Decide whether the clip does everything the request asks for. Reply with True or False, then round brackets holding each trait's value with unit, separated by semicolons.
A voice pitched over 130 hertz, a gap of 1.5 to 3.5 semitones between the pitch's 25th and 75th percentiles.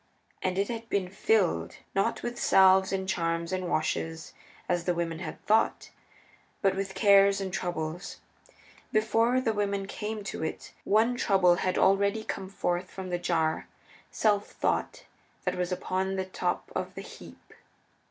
True (190 Hz; 2.5 semitones)